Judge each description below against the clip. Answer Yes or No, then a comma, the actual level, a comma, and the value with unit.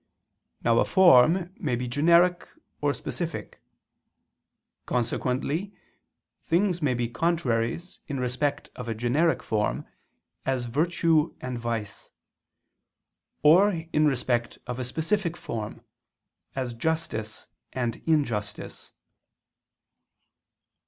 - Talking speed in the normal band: No, slow, 100 wpm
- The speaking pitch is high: No, low, 135 Hz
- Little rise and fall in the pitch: No, wide, 5.6 semitones